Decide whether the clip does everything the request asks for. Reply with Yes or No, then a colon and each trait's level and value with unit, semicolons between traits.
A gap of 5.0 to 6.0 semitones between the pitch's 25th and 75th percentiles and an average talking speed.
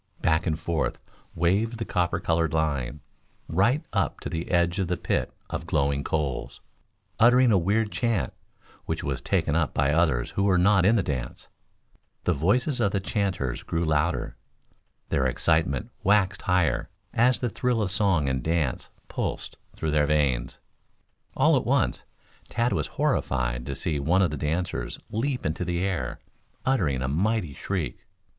Yes: average, 5.3 semitones; average, 165 wpm